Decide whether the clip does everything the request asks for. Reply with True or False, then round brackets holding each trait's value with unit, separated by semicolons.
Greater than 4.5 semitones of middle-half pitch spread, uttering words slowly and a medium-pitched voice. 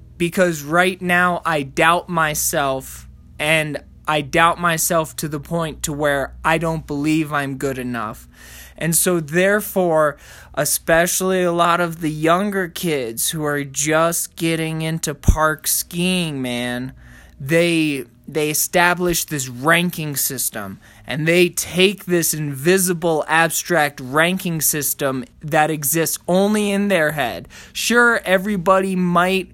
False (3.4 semitones; 125 wpm; 160 Hz)